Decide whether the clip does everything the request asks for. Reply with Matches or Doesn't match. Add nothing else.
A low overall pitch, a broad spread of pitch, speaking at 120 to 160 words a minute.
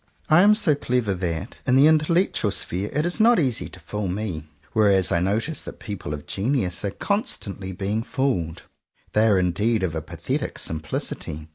Doesn't match